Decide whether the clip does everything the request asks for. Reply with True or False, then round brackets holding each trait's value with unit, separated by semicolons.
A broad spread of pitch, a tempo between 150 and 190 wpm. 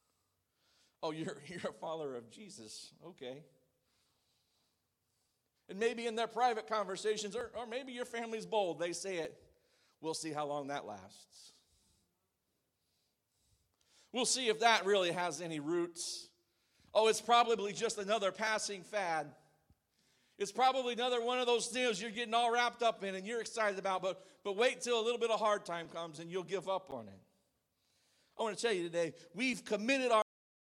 True (5.7 semitones; 170 wpm)